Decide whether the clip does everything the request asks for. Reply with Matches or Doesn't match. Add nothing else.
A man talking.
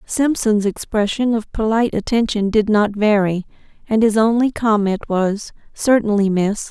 Doesn't match